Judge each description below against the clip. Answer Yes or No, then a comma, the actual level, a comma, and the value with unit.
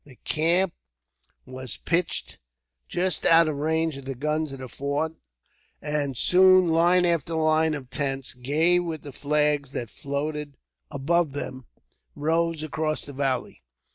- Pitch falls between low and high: Yes, medium, 150 Hz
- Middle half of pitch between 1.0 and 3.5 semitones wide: Yes, average, 2.9 semitones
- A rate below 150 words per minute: Yes, average, 140 wpm